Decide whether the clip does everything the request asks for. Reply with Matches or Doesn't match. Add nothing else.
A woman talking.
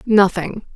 Matches